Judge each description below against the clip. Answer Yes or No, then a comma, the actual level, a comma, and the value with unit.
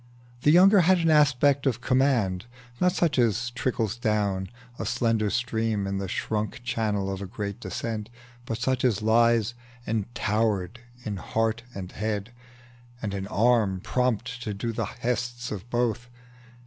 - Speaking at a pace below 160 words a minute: Yes, average, 150 wpm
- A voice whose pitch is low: Yes, low, 115 Hz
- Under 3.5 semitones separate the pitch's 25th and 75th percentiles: Yes, average, 3.0 semitones